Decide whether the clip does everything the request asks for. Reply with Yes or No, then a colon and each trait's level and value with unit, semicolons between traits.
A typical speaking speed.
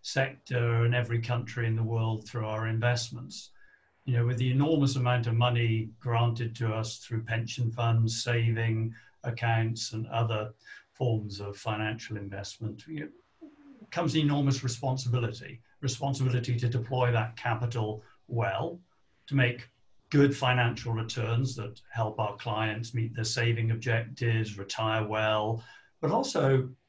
No: slow, 130 wpm